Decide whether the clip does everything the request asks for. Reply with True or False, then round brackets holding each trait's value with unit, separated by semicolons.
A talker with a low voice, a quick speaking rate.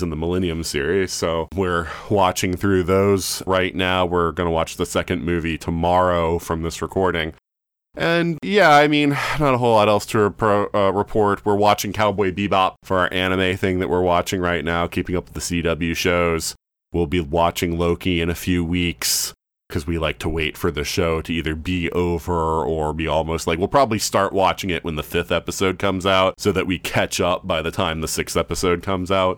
True (90 Hz; 210 wpm)